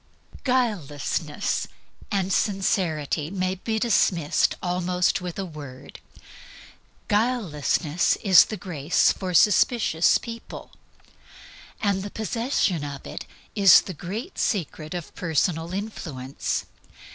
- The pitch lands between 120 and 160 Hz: No, medium, 180 Hz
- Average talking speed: No, slow, 100 wpm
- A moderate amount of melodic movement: Yes, average, 4.7 semitones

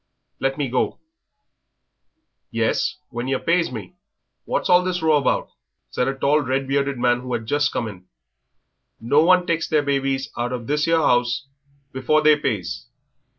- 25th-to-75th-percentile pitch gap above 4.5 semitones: No, average, 3.7 semitones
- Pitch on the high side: No, low, 135 Hz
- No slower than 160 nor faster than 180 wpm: Yes, average, 165 wpm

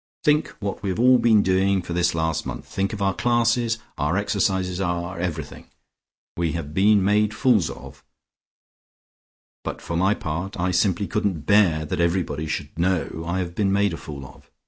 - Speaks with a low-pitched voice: Yes, very low, 95 Hz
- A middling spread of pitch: Yes, average, 3.3 semitones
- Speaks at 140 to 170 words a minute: No, average, 180 wpm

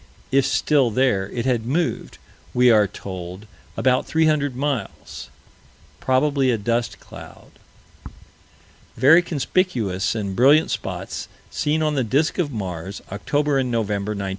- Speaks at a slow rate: Yes, slow, 130 wpm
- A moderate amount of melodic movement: No, wide, 5.7 semitones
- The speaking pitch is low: Yes, low, 125 Hz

